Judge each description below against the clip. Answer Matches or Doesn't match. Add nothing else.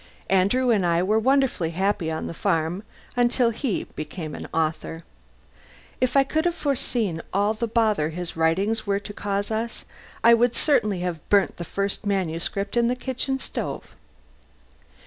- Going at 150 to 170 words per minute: Matches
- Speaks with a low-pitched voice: Doesn't match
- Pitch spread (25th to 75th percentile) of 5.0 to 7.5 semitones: Matches